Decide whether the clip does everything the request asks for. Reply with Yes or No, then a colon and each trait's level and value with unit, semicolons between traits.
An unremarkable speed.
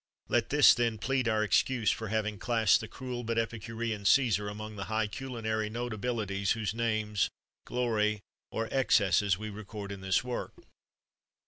Yes: average, 150 wpm